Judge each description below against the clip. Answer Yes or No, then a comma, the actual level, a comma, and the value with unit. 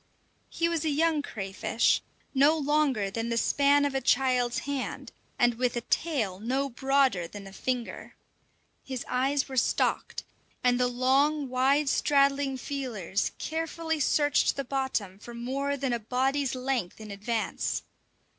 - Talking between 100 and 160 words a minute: Yes, average, 145 wpm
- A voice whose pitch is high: Yes, very high, 265 Hz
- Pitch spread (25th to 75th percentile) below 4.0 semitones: Yes, average, 3.0 semitones